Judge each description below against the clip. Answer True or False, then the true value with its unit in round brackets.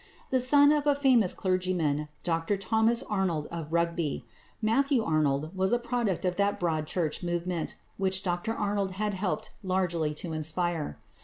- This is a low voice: False (185 Hz)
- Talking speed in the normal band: True (155 wpm)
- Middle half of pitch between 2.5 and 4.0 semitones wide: False (4.5 semitones)